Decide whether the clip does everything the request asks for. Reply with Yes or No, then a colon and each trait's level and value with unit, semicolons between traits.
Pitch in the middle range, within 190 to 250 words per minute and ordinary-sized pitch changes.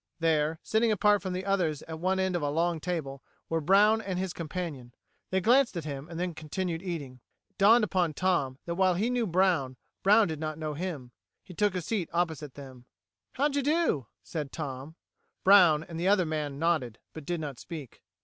Yes: medium, 170 Hz; average, 200 wpm; average, 4.0 semitones